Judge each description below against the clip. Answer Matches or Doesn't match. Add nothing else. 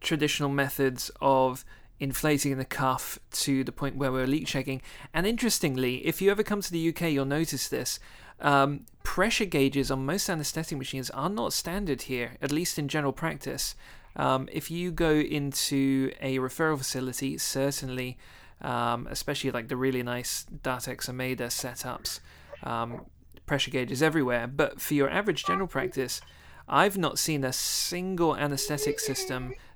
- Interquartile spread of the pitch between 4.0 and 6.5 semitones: Doesn't match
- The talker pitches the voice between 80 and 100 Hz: Doesn't match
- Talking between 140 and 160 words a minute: Matches